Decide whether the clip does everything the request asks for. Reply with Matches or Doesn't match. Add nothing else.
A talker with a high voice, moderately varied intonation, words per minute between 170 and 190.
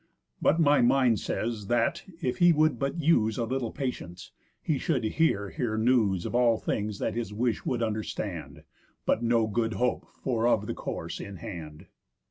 Doesn't match